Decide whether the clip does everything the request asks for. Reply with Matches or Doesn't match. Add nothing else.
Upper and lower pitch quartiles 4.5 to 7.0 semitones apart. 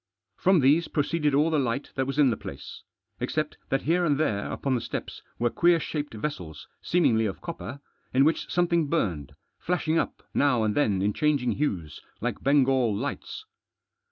Matches